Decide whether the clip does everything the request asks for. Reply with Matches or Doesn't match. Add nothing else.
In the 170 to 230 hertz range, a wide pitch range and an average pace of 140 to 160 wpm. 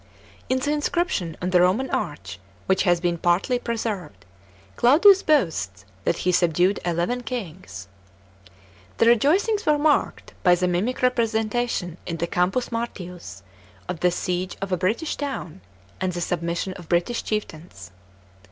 Matches